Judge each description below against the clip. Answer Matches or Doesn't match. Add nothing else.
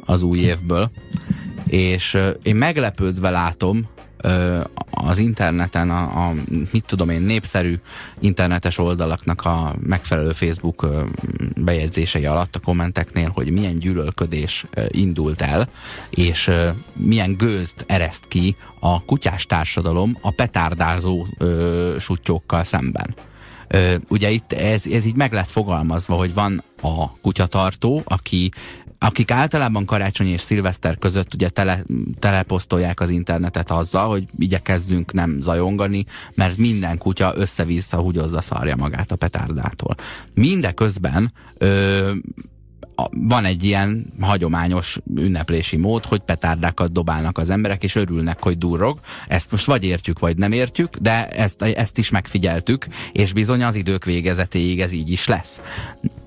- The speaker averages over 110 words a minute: Matches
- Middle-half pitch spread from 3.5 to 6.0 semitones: Doesn't match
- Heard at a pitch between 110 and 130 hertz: Doesn't match